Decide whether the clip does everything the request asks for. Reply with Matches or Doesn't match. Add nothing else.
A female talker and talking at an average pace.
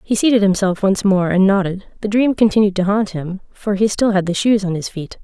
Doesn't match